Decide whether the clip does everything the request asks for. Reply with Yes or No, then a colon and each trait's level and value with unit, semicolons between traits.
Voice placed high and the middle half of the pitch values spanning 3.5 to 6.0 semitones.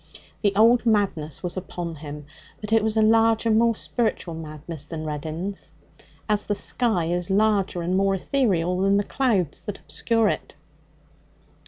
Yes: high, 195 Hz; average, 4.7 semitones